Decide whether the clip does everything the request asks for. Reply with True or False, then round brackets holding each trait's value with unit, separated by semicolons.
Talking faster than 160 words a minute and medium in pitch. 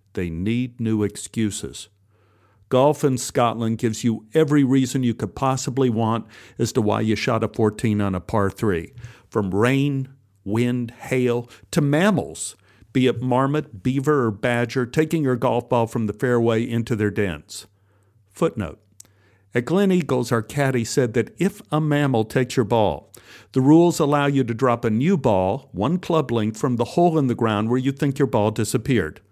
False (175 wpm; 120 Hz)